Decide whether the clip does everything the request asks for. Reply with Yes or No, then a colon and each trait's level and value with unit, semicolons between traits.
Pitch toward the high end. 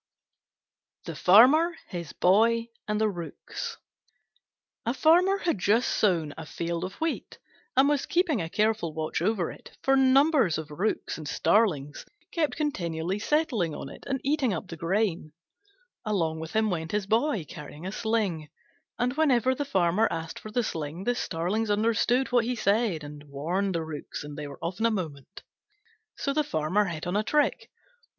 Yes: high, 205 Hz